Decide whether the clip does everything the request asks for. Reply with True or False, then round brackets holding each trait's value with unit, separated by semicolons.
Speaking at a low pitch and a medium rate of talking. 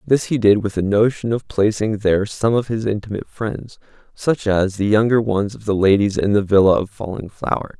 False (105 Hz; 215 wpm)